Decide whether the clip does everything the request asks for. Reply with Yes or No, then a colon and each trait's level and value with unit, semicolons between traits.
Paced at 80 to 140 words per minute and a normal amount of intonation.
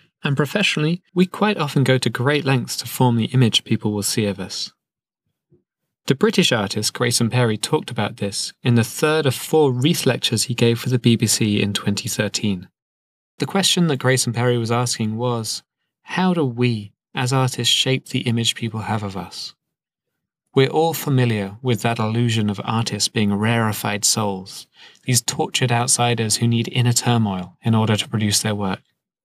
No: average, 170 wpm; average, 3.6 semitones